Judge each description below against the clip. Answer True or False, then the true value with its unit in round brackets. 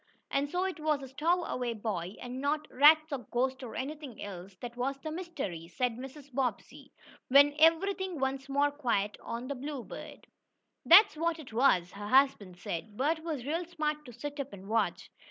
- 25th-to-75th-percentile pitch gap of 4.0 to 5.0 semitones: True (4.4 semitones)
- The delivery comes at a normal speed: True (180 wpm)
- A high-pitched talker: True (275 Hz)